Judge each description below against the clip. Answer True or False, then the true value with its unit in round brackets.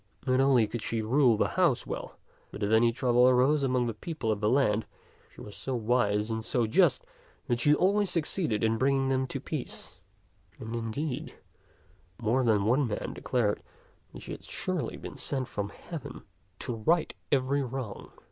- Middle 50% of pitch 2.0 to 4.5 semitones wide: True (3.6 semitones)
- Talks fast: False (175 wpm)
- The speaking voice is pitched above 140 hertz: False (125 Hz)